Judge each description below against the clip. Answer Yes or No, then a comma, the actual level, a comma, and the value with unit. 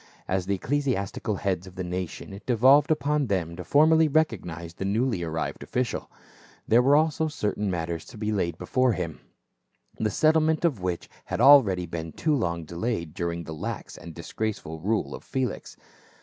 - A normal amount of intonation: No, wide, 7.7 semitones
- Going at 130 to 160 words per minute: No, average, 170 wpm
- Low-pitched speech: Yes, low, 100 Hz